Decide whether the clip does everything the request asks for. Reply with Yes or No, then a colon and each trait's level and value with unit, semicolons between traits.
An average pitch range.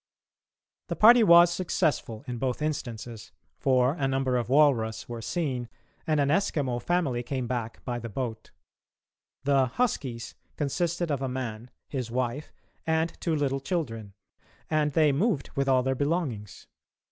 Yes: average, 4.4 semitones